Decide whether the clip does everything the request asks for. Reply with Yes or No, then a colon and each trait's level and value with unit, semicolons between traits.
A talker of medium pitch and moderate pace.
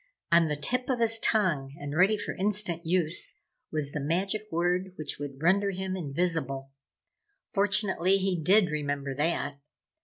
Yes: medium, 175 Hz; average, 150 wpm